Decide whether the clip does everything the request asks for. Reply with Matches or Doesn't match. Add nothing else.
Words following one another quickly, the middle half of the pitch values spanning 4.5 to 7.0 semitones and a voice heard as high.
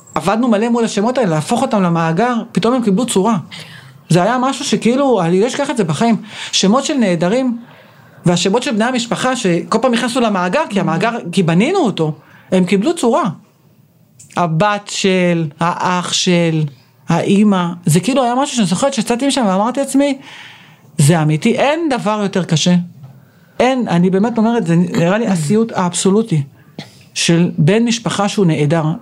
Matches